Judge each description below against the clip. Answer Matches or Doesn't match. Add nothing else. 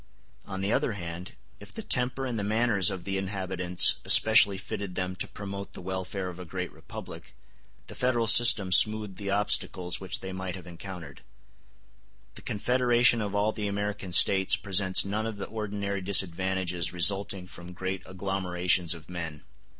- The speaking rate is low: Doesn't match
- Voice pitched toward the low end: Matches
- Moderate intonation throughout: Doesn't match